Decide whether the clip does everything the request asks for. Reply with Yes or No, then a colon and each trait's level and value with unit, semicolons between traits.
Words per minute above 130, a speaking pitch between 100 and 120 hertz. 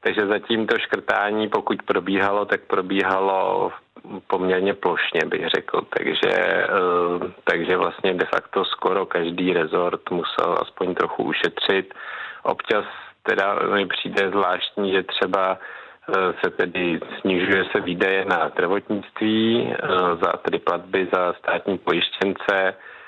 No: slow, 115 wpm; low, 105 Hz